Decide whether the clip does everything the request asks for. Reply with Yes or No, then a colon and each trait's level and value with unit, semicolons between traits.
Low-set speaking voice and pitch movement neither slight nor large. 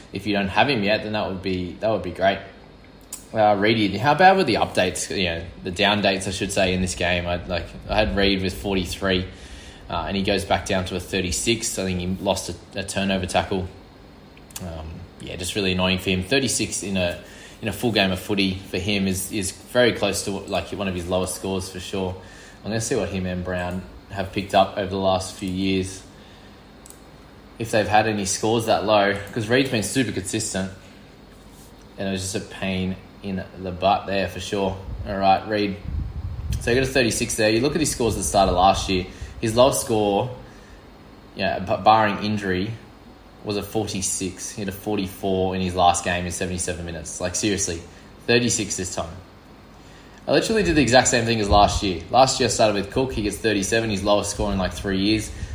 No: very low, 95 Hz; narrow, 2.3 semitones